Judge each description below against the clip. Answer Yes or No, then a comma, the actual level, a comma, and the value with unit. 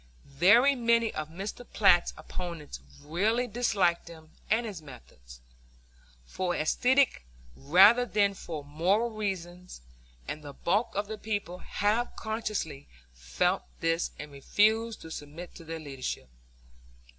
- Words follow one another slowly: Yes, slow, 125 wpm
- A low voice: No, medium, 180 Hz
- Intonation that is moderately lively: No, wide, 5.9 semitones